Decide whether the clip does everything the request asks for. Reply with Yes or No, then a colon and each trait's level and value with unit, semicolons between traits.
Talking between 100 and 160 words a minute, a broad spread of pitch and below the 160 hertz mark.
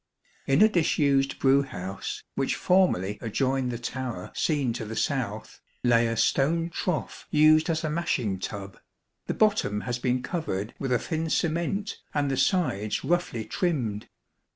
Yes: average, 150 wpm; wide, 6.2 semitones; low, 135 Hz